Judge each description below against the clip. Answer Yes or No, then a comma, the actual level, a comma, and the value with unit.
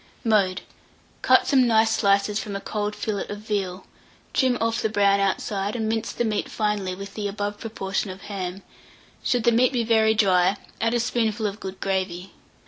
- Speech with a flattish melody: Yes, narrow, 2.2 semitones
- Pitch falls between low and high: No, high, 210 Hz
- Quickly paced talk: No, average, 185 wpm